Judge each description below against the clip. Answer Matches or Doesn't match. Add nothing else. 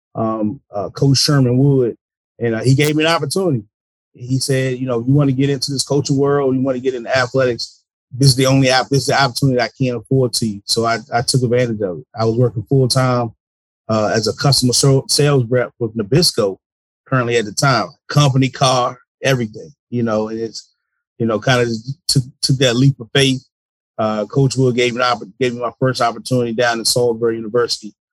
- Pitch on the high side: Doesn't match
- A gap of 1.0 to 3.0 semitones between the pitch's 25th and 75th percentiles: Matches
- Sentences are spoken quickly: Matches